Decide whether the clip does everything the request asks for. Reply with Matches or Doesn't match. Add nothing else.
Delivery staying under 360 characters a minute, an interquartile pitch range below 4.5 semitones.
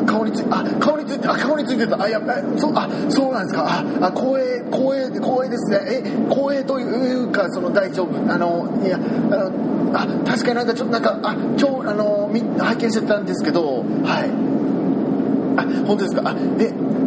Matches